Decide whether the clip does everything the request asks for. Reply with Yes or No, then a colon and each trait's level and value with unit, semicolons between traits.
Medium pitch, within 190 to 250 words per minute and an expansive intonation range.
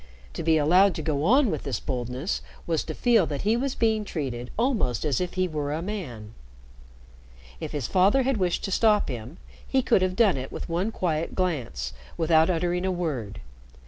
Yes: medium, 170 Hz; average, 195 wpm; wide, 5.8 semitones